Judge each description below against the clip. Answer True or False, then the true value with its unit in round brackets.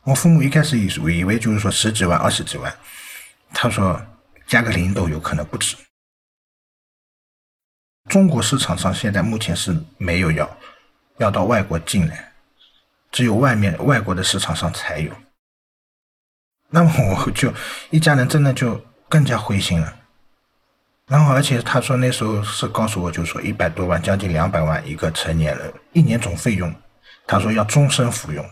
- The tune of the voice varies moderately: False (6.9 semitones)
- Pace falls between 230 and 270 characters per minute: True (245 characters per minute)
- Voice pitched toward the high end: False (110 Hz)